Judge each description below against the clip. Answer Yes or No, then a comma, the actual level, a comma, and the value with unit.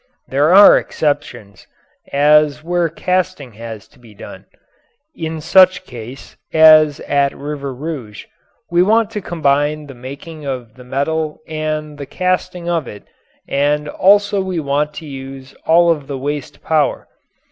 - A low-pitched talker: No, medium, 150 Hz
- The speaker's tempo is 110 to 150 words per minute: Yes, average, 145 wpm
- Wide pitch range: No, average, 3.4 semitones